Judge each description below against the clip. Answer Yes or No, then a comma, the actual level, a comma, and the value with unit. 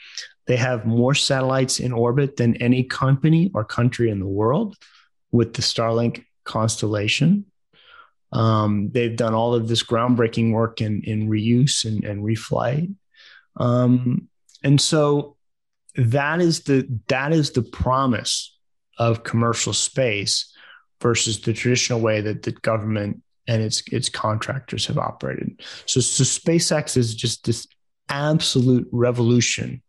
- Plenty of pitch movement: No, average, 3.0 semitones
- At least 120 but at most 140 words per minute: Yes, slow, 135 wpm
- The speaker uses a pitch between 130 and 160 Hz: No, low, 120 Hz